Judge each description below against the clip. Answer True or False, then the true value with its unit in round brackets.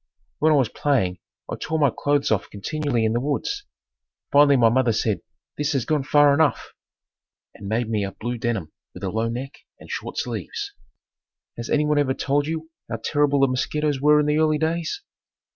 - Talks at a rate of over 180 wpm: True (190 wpm)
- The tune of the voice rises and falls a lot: False (4.3 semitones)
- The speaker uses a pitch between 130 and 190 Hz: True (140 Hz)